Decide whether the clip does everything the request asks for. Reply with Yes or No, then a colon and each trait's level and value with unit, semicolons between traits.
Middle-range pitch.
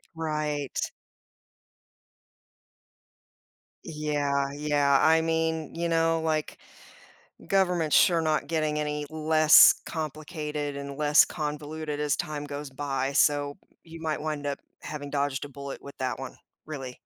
Yes: medium, 150 Hz